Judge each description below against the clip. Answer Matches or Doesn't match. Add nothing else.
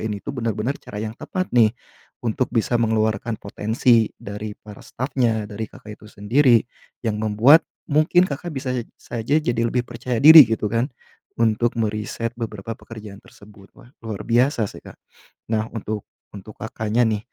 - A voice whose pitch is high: Doesn't match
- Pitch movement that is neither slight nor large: Doesn't match